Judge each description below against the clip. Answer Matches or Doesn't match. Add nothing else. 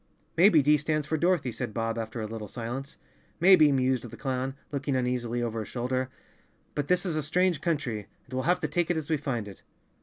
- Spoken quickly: Matches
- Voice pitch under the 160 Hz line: Matches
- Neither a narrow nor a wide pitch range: Matches